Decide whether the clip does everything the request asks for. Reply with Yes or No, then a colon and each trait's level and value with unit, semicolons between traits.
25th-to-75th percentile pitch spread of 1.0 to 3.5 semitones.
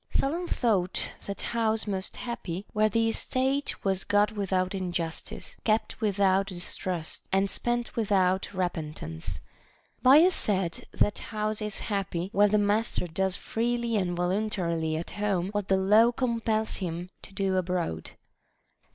Yes: average, 3.1 semitones